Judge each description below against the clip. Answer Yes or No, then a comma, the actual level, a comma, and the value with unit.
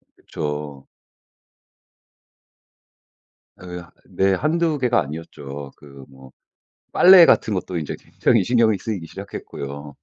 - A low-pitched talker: Yes, very low, 85 Hz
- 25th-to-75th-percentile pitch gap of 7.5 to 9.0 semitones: Yes, wide, 8.2 semitones